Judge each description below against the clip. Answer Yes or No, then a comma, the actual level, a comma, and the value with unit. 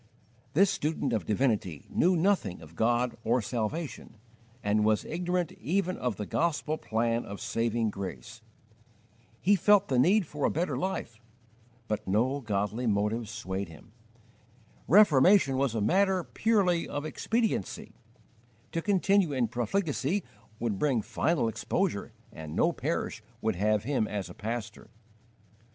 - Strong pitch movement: Yes, wide, 8.0 semitones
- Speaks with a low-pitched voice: Yes, low, 125 Hz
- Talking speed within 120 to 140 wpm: Yes, slow, 135 wpm